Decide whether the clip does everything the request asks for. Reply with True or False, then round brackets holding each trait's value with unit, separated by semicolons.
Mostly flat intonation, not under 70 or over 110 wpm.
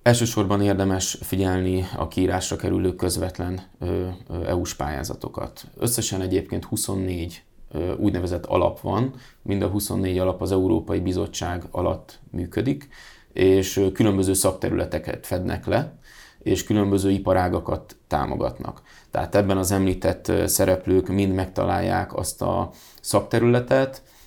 True (1.8 semitones; 105 wpm)